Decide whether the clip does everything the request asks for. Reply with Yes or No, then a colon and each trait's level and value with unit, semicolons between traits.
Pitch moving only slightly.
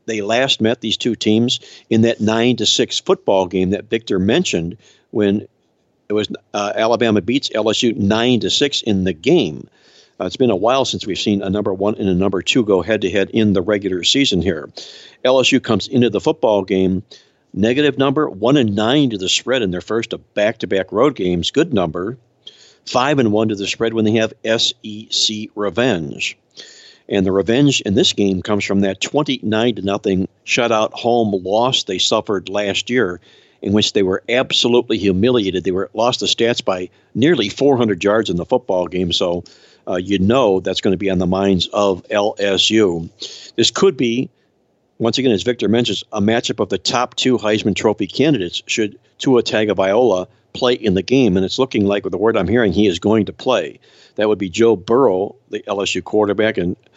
No: average, 3.3 semitones